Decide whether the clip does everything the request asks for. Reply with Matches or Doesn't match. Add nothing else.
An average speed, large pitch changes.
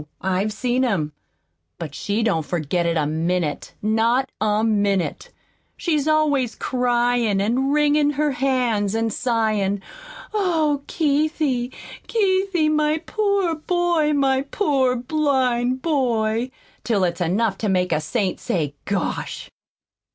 Doesn't match